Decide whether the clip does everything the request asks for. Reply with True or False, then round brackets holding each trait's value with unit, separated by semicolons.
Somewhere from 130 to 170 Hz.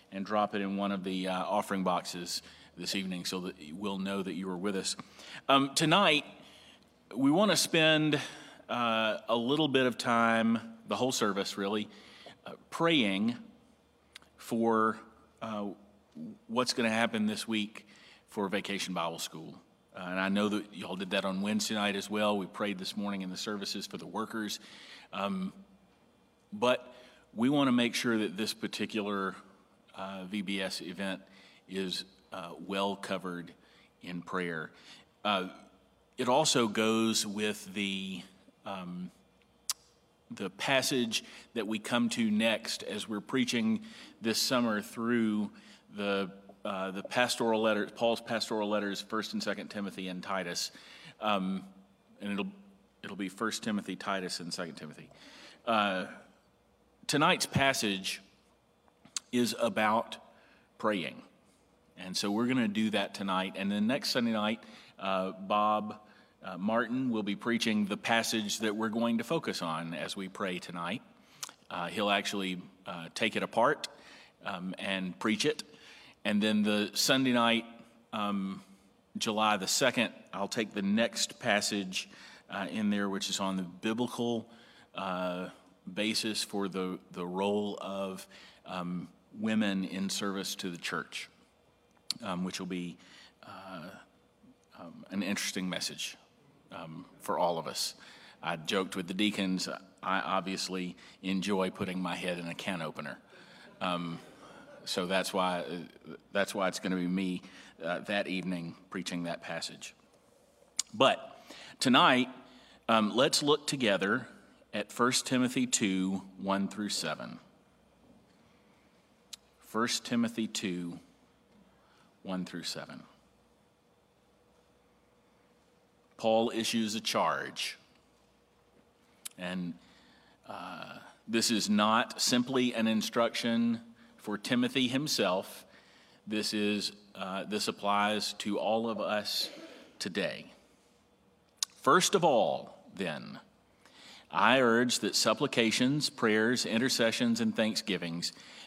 False (105 Hz)